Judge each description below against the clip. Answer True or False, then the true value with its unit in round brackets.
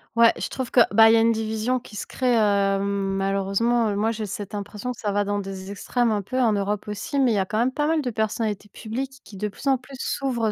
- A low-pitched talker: False (215 Hz)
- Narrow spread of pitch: False (3.3 semitones)